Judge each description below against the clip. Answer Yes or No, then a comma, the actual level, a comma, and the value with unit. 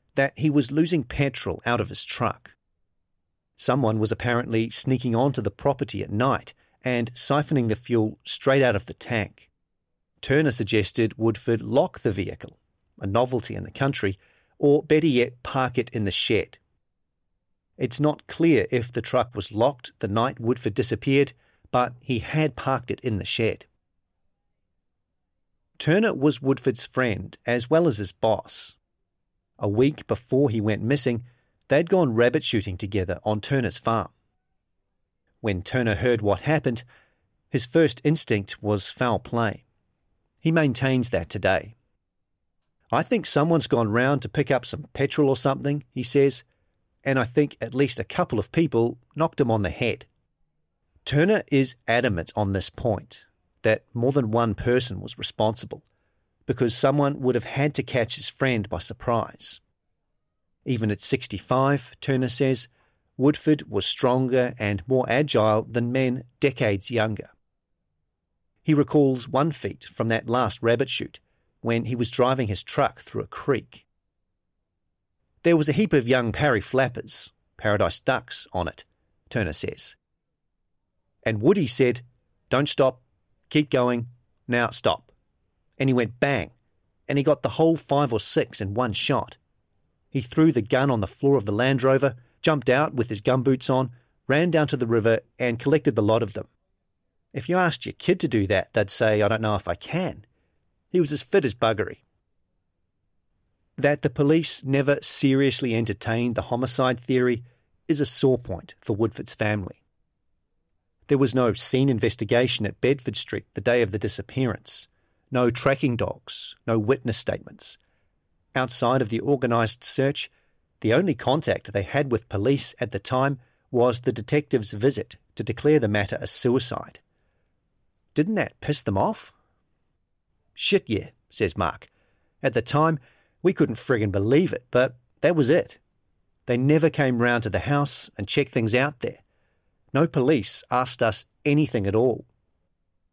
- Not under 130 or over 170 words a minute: Yes, average, 160 wpm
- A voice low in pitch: Yes, low, 120 Hz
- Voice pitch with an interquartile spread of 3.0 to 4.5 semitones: No, average, 4.9 semitones